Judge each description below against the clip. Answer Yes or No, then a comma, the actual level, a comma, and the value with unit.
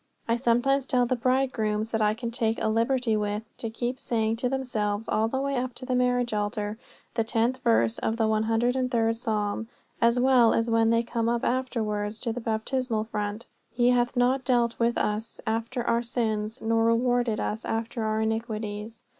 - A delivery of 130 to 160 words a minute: No, average, 185 wpm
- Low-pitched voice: No, high, 230 Hz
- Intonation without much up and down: Yes, narrow, 2.0 semitones